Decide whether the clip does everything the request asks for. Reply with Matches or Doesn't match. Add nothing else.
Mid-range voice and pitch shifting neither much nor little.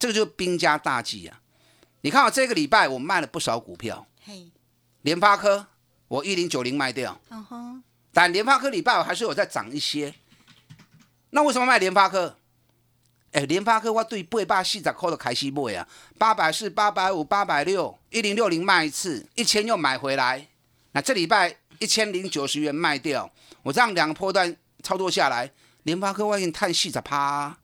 Doesn't match